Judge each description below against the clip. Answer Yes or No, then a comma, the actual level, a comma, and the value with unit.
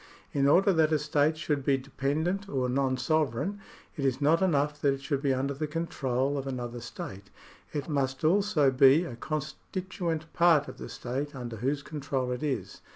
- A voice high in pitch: No, medium, 145 Hz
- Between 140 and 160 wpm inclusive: No, average, 185 wpm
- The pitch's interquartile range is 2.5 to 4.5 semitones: Yes, average, 2.9 semitones